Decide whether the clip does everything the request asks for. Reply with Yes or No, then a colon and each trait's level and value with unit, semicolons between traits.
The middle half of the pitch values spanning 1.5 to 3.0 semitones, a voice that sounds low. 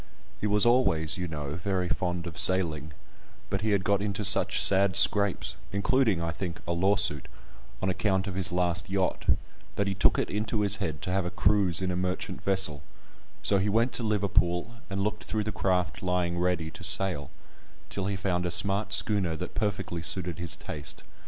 Yes: narrow, 2.5 semitones; very low, 95 Hz